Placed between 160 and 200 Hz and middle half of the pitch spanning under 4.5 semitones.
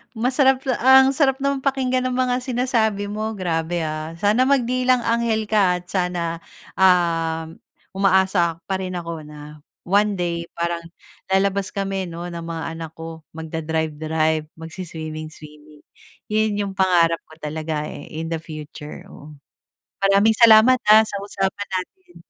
No: medium, 185 Hz; average, 5.2 semitones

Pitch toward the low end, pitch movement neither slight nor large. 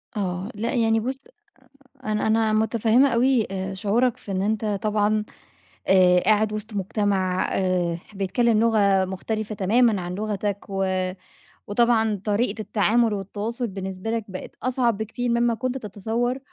No: high, 215 Hz; average, 3.0 semitones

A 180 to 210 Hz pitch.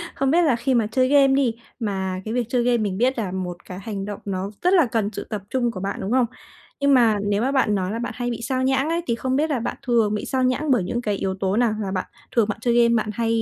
No: high, 235 Hz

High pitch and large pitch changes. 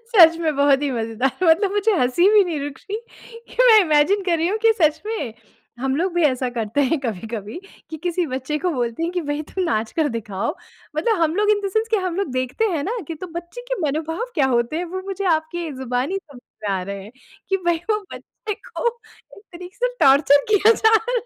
Yes: very high, 320 Hz; wide, 6.5 semitones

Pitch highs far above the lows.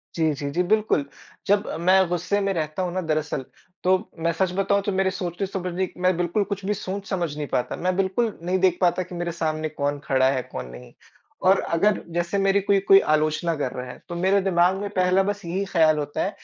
No: average, 3.6 semitones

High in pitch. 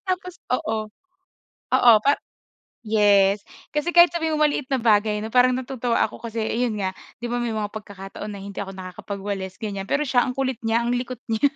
Yes: high, 225 Hz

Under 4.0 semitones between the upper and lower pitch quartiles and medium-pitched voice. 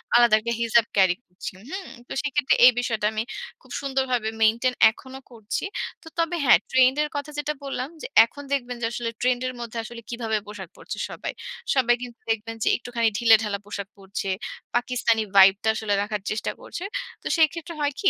No: average, 3.0 semitones; high, 235 Hz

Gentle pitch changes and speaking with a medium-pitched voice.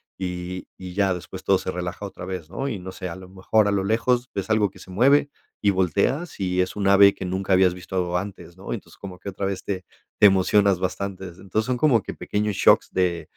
No: narrow, 1.9 semitones; very low, 95 Hz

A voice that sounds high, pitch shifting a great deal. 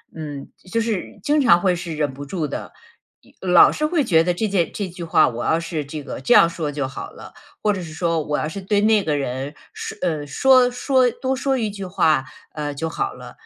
No: medium, 170 Hz; wide, 6.0 semitones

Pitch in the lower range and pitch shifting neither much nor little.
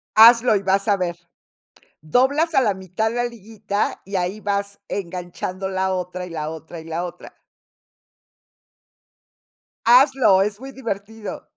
No: high, 200 Hz; average, 3.7 semitones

